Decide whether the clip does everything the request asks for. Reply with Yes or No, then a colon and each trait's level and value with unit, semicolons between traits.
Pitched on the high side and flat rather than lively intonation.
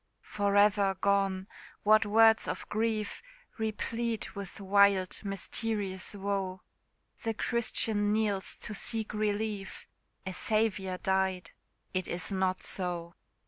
Yes: high, 200 Hz; narrow, 2.2 semitones